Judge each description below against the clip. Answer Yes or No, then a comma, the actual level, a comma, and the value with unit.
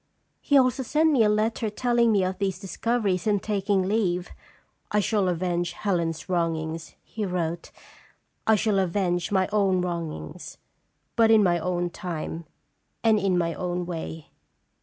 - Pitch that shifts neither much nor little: Yes, average, 3.5 semitones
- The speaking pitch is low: No, medium, 185 Hz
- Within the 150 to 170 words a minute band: Yes, average, 160 wpm